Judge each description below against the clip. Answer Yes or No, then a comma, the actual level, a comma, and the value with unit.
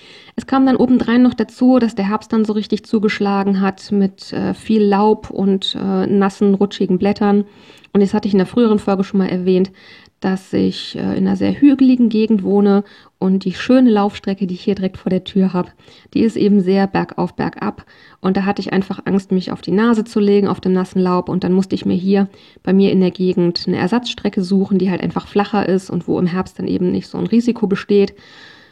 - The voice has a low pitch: No, high, 200 Hz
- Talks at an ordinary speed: No, fast, 225 wpm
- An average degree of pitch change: No, narrow, 2.2 semitones